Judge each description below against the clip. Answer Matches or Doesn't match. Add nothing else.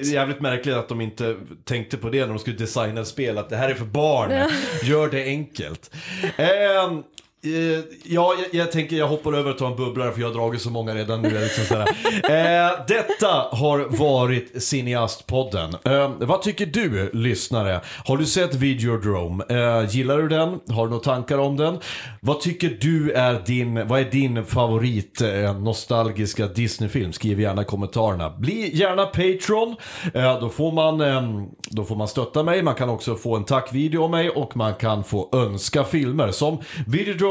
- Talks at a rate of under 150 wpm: Doesn't match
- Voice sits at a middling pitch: Doesn't match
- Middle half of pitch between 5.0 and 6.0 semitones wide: Matches